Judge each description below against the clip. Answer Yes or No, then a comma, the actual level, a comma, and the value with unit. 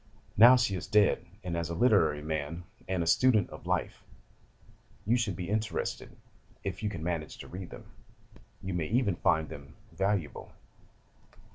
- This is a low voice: Yes, very low, 90 Hz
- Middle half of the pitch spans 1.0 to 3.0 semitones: No, average, 4.3 semitones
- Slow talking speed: No, average, 160 wpm